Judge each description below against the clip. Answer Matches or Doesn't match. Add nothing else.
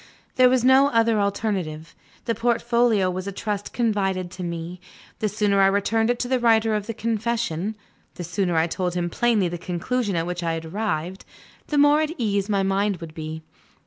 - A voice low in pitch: Doesn't match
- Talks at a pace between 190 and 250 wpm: Matches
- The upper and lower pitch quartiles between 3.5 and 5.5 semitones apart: Matches